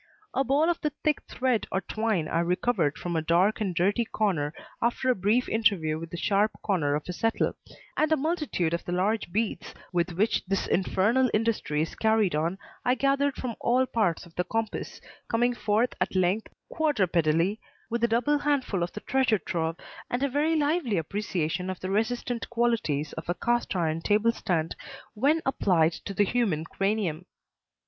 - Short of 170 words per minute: No, average, 180 wpm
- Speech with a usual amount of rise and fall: No, wide, 5.7 semitones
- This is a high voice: Yes, high, 210 Hz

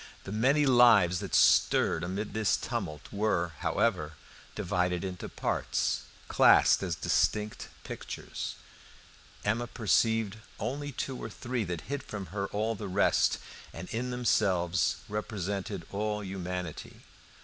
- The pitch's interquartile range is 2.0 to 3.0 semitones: No, average, 3.8 semitones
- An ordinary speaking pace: No, slow, 125 wpm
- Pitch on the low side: Yes, low, 105 Hz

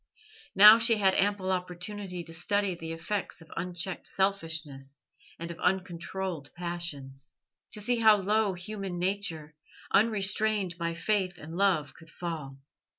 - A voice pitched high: No, medium, 180 Hz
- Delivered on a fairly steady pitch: No, average, 3.5 semitones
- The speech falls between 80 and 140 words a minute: Yes, slow, 135 wpm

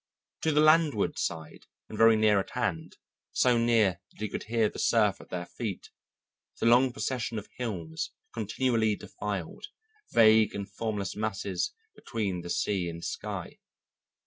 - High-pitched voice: No, low, 110 Hz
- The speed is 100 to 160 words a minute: Yes, average, 150 wpm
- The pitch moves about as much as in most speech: Yes, average, 3.3 semitones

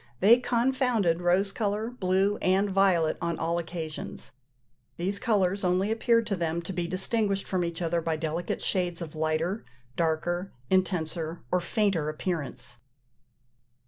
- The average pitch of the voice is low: No, medium, 180 Hz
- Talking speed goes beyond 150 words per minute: No, average, 140 wpm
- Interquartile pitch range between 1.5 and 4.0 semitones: Yes, average, 3.1 semitones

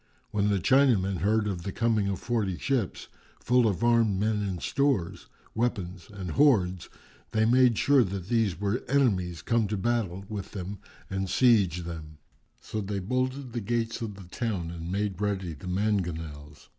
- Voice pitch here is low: Yes, low, 100 Hz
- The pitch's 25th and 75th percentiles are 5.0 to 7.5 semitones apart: No, average, 4.2 semitones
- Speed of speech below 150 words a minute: No, average, 170 wpm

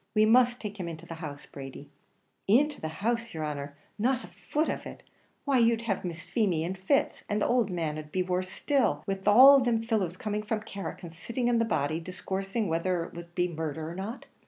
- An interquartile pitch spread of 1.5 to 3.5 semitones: No, wide, 5.6 semitones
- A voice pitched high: Yes, high, 195 Hz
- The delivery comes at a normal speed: No, fast, 220 wpm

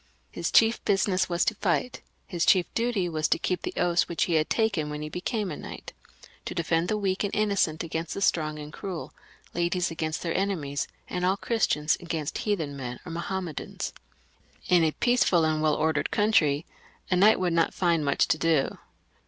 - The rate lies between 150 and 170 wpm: No, average, 190 wpm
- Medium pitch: Yes, medium, 170 Hz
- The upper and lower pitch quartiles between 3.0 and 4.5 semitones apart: Yes, average, 3.6 semitones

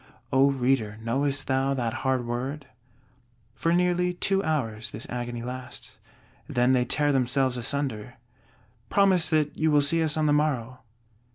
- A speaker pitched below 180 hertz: Yes, low, 135 Hz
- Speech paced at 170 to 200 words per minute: No, average, 150 wpm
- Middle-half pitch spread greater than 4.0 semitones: No, average, 3.6 semitones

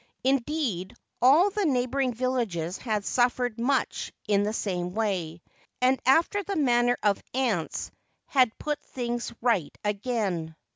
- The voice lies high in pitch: Yes, high, 240 Hz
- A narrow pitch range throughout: No, average, 4.6 semitones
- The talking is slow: Yes, slow, 130 wpm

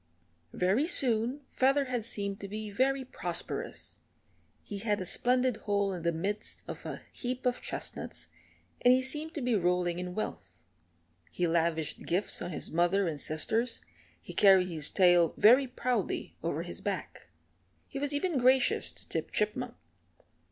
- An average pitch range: No, wide, 6.0 semitones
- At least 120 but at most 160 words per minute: Yes, average, 155 wpm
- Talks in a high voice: Yes, high, 210 Hz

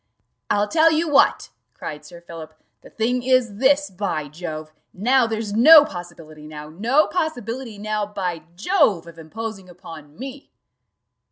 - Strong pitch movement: Yes, wide, 7.4 semitones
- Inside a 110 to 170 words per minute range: Yes, average, 145 wpm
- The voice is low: No, high, 205 Hz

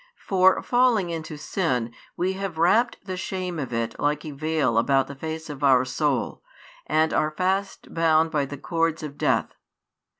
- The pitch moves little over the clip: No, average, 4.5 semitones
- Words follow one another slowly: No, average, 170 wpm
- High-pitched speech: No, medium, 160 Hz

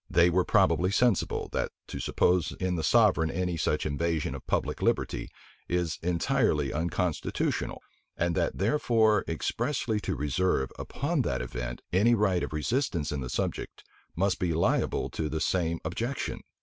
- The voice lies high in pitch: No, very low, 90 Hz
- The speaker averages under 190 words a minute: Yes, average, 150 wpm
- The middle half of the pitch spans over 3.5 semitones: Yes, average, 4.5 semitones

